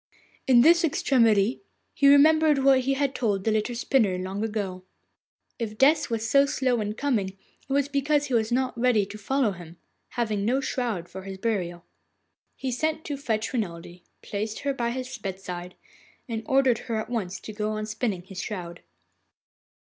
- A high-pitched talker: Yes, high, 230 Hz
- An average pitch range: Yes, average, 5.0 semitones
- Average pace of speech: Yes, average, 175 wpm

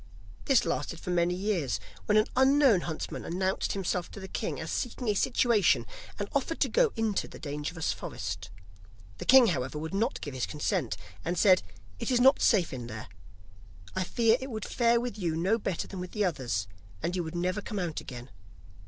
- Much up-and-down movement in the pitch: Yes, wide, 5.9 semitones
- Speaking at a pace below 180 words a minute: No, average, 195 wpm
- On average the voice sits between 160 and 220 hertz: Yes, medium, 185 Hz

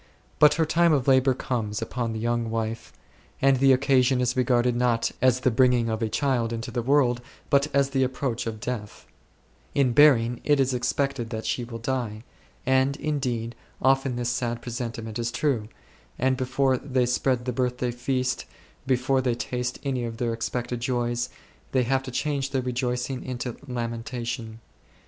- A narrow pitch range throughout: Yes, narrow, 2.0 semitones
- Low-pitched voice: Yes, low, 125 Hz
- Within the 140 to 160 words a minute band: No, average, 170 wpm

